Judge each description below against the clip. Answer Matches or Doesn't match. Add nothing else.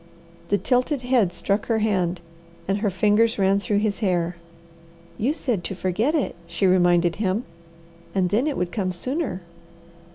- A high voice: Matches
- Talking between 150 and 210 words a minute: Matches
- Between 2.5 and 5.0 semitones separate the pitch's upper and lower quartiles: Matches